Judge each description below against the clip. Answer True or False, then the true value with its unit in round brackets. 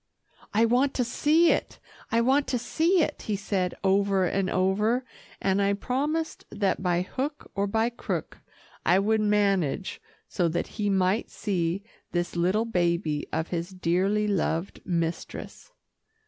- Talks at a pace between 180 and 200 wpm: False (150 wpm)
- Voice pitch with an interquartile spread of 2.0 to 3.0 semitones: False (4.2 semitones)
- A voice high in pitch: True (200 Hz)